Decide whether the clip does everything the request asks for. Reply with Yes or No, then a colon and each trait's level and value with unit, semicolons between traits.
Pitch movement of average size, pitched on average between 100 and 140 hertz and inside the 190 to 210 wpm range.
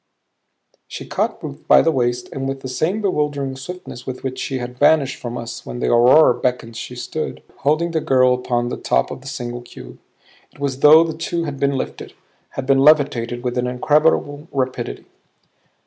Yes: average, 3.3 semitones; low, 135 Hz; average, 195 wpm